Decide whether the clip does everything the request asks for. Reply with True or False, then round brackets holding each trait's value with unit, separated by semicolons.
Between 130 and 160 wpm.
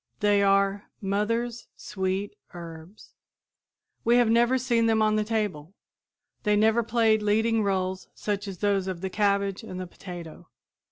True (150 wpm)